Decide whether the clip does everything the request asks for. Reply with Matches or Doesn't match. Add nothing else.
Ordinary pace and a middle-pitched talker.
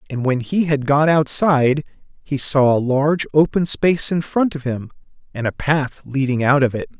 Matches